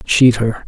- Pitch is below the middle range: Yes, low, 115 Hz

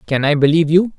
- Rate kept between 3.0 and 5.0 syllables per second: No, 7.3 syllables/s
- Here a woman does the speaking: No, male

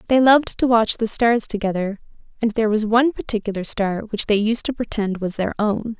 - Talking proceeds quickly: Yes, fast, 210 wpm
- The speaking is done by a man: No, female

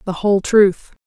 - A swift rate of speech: No, average, 170 wpm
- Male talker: No, female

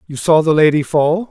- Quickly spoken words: Yes, fast, 230 wpm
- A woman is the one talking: No, male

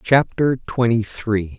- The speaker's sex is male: Yes, male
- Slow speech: Yes, slow, 115 wpm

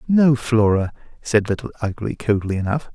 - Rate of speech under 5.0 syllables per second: No, 5.1 syllables/s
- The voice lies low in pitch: Yes, low, 115 Hz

